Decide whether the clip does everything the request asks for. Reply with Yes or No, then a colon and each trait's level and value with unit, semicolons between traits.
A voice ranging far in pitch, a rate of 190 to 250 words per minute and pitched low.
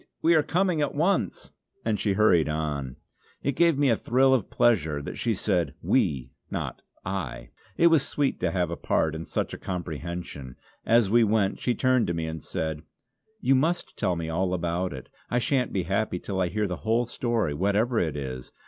Yes: wide, 6.9 semitones; average, 200 wpm; very low, 95 Hz